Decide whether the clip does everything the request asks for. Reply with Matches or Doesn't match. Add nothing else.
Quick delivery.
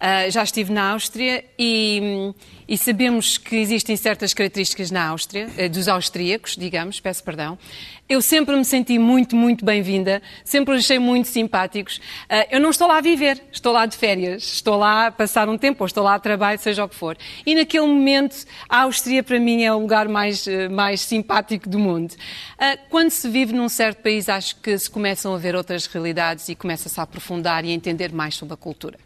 Matches